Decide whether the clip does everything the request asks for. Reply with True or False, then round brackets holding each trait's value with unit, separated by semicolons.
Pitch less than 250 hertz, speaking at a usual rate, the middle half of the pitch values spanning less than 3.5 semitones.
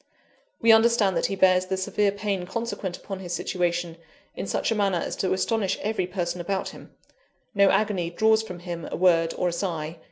True (190 Hz; 195 wpm; 2.9 semitones)